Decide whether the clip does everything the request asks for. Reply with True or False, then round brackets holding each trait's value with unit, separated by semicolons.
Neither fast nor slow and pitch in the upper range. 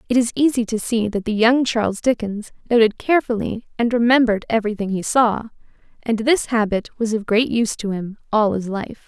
True (190 wpm; 225 Hz)